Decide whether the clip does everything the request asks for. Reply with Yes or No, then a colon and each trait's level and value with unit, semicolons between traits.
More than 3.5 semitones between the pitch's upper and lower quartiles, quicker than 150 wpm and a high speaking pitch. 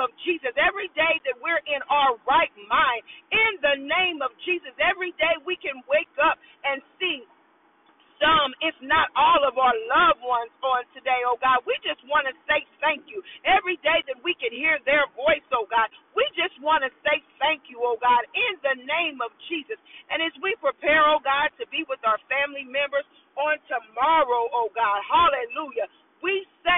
Yes: average, 3.9 semitones; average, 185 wpm; very high, 300 Hz